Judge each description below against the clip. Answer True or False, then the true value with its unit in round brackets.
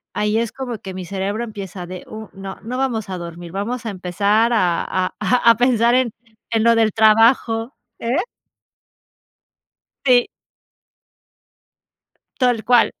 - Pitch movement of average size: True (3.6 semitones)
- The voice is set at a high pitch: True (220 Hz)